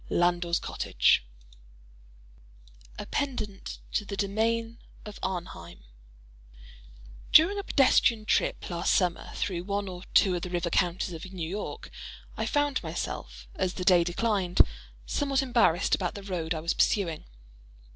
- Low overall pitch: No, medium, 185 Hz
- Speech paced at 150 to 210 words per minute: No, slow, 135 wpm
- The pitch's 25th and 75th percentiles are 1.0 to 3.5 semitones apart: No, average, 3.9 semitones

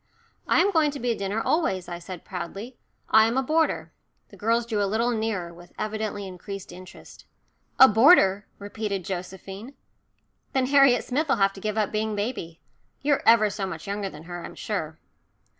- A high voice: Yes, high, 210 Hz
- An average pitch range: Yes, average, 4.0 semitones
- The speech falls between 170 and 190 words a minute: Yes, average, 180 wpm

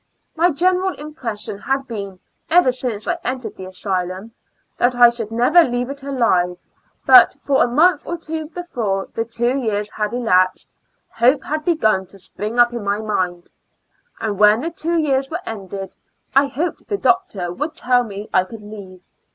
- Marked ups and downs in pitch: Yes, wide, 6.4 semitones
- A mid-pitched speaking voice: No, high, 240 Hz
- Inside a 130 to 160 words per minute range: No, average, 175 wpm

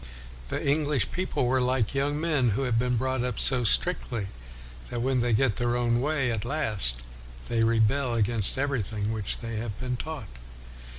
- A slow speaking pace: No, average, 175 wpm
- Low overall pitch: Yes, low, 120 Hz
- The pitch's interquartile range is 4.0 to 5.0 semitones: No, average, 3.2 semitones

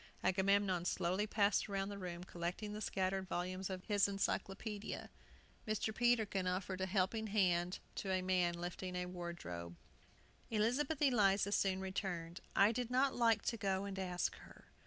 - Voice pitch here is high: Yes, high, 195 Hz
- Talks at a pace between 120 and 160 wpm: Yes, average, 155 wpm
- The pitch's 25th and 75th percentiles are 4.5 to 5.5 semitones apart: No, narrow, 2.5 semitones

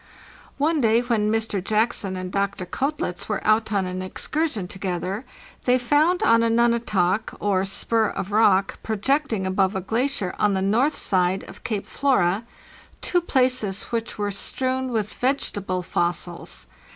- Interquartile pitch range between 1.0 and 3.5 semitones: No, average, 4.5 semitones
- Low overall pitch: No, high, 215 Hz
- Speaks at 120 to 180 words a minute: Yes, average, 155 wpm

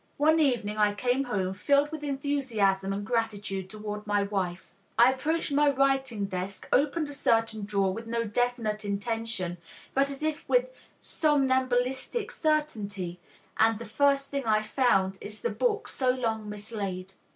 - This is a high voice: Yes, high, 230 Hz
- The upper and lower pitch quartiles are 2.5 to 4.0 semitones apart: No, average, 5.3 semitones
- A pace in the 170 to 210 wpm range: No, average, 150 wpm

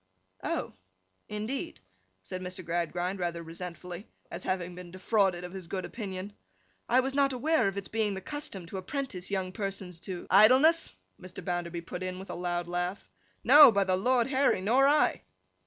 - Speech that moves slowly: No, average, 170 wpm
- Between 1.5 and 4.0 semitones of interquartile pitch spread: No, average, 4.4 semitones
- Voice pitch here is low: No, high, 190 Hz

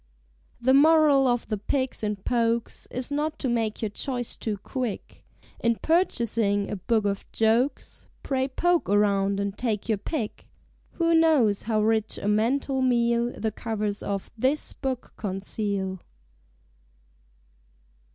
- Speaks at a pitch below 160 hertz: No, high, 230 Hz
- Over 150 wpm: No, slow, 135 wpm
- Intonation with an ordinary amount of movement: Yes, average, 4.1 semitones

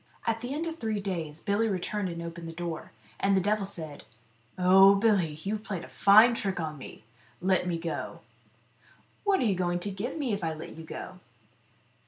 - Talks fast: Yes, fast, 210 wpm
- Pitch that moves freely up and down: No, average, 4.0 semitones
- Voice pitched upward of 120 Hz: Yes, high, 190 Hz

